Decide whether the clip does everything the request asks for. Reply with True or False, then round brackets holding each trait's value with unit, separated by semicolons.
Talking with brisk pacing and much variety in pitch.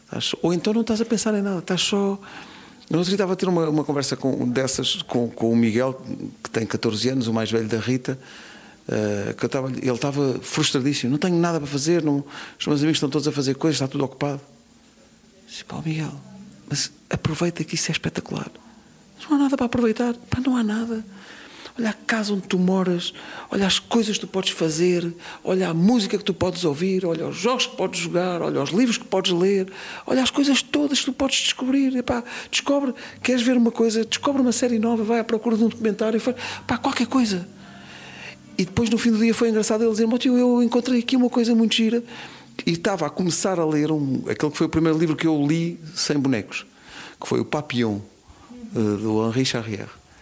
True (215 wpm; 8.0 semitones)